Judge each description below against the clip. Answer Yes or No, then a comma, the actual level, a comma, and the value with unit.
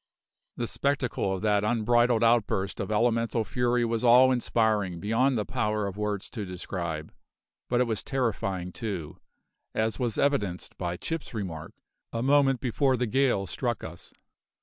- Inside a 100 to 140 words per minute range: No, average, 150 wpm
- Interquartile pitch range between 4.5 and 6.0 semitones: No, average, 3.9 semitones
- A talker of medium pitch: No, low, 115 Hz